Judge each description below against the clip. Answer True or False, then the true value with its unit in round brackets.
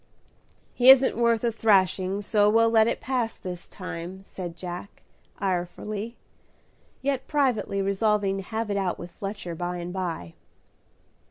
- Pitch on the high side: True (200 Hz)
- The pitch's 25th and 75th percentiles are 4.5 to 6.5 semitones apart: False (3.8 semitones)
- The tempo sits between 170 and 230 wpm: False (145 wpm)